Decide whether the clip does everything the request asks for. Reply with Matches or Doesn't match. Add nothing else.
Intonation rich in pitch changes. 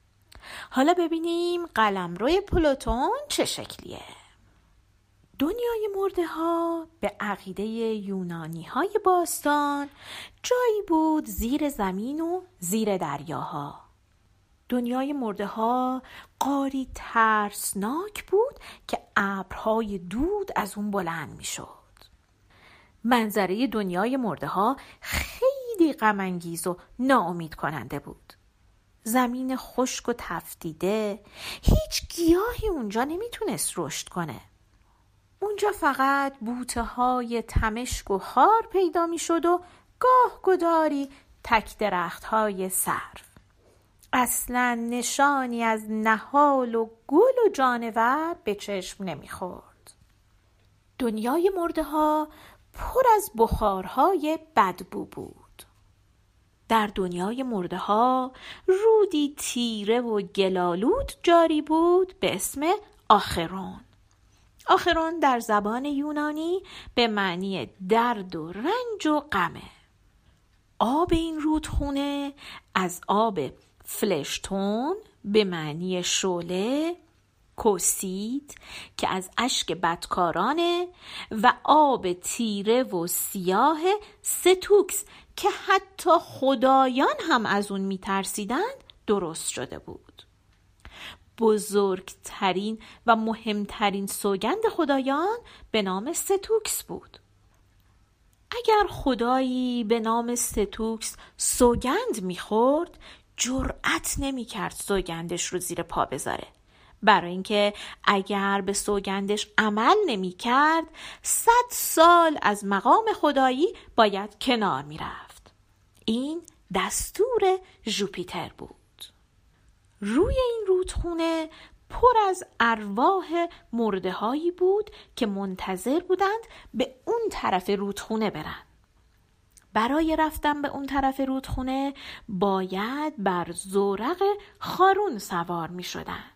Matches